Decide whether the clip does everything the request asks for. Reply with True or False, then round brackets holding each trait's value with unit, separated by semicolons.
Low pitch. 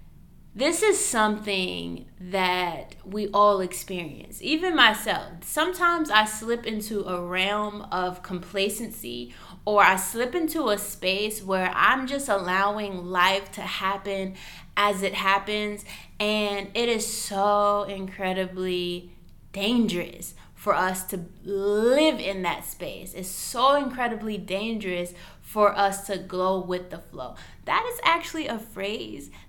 False (200 Hz)